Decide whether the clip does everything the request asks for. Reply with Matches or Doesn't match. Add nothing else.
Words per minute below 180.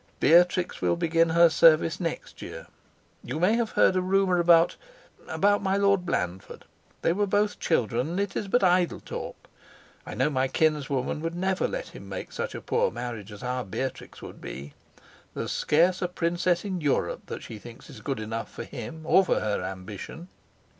Doesn't match